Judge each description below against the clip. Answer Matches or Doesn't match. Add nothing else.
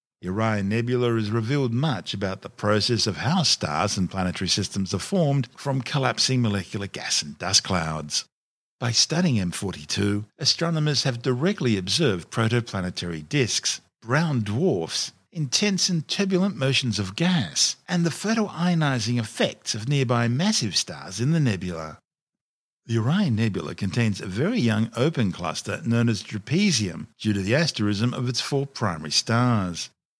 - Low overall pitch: Matches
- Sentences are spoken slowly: Doesn't match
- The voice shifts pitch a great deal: Matches